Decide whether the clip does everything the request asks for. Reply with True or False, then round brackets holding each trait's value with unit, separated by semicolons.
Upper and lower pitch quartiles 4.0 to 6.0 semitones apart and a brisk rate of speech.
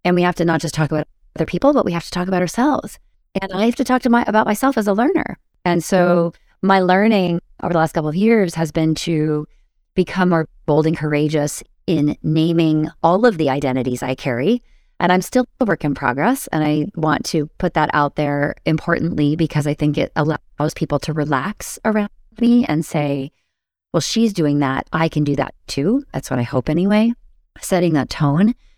True (4.5 semitones; 210 wpm)